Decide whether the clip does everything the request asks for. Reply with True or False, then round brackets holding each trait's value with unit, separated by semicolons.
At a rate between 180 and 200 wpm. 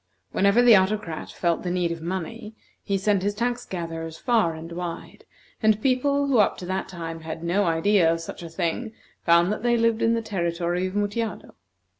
True (195 wpm)